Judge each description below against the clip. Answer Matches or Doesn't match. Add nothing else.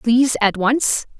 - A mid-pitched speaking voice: Doesn't match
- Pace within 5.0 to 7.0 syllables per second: Doesn't match